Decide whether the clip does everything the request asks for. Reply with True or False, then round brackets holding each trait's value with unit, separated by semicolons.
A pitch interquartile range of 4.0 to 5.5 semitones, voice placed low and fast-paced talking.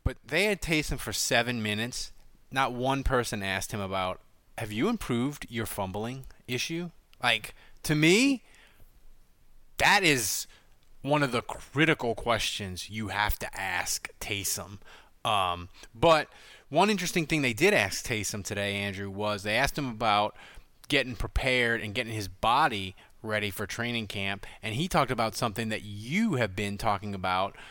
False (4.9 semitones; 115 Hz; 155 wpm)